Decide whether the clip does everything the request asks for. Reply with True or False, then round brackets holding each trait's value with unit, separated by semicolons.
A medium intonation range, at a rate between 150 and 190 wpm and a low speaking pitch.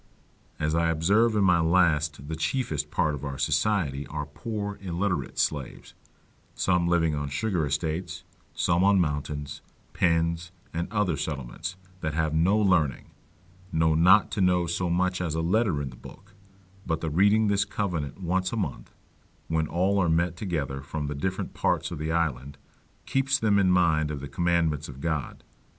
True (3.6 semitones; 170 wpm; 85 Hz)